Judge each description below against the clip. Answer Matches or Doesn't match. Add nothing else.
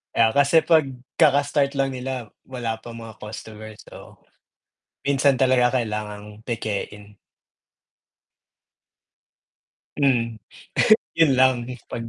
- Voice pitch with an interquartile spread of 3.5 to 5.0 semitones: Matches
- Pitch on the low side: Matches